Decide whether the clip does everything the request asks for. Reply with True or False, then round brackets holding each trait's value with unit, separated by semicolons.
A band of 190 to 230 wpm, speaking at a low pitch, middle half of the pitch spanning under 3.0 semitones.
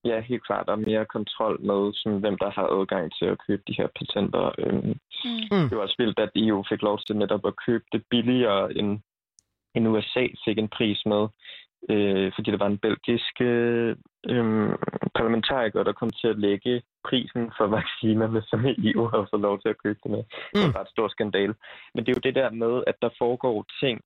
True (195 wpm; 110 Hz; 2.5 semitones)